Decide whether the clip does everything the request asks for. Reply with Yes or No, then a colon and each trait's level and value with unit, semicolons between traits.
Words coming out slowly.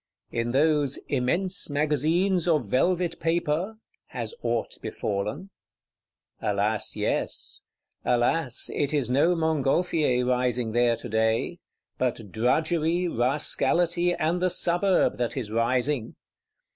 Yes: slow, 105 wpm